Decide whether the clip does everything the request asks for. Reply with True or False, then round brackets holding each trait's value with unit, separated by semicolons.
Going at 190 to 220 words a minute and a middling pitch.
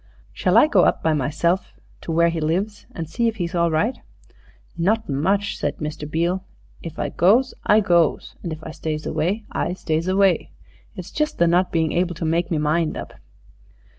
True (195 wpm; 170 Hz)